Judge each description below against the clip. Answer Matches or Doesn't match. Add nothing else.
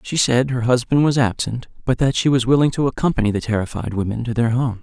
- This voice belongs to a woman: Doesn't match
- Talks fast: Matches